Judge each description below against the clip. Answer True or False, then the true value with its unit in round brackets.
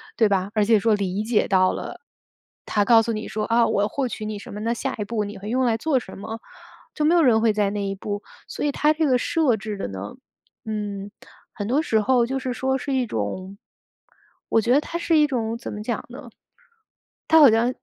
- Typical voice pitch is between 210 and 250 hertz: True (220 Hz)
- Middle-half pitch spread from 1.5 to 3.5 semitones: False (4.0 semitones)